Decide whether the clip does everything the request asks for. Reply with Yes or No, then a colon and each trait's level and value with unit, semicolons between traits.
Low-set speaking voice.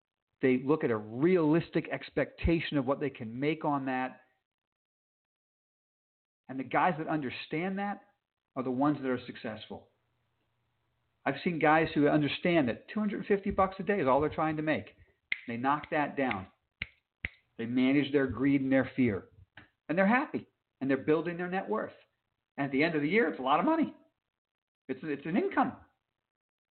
No: medium, 145 Hz